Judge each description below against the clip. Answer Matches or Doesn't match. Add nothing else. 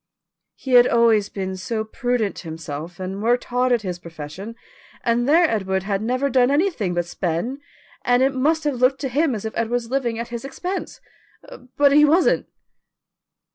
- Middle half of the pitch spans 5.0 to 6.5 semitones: Matches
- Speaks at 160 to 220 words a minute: Matches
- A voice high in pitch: Matches